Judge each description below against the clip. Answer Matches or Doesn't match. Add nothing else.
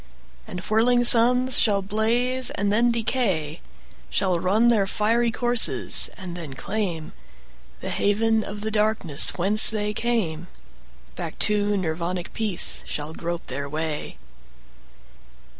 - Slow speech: Matches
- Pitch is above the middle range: Matches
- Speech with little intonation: Doesn't match